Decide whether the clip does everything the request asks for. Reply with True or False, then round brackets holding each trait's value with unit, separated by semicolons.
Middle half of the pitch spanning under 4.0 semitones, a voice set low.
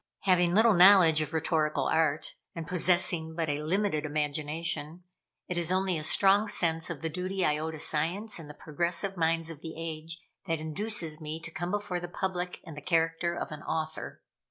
False (2.5 semitones; 165 Hz)